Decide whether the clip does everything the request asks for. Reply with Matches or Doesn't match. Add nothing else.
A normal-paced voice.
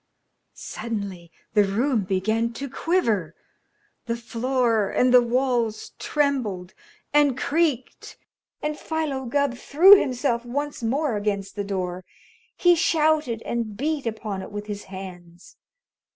Doesn't match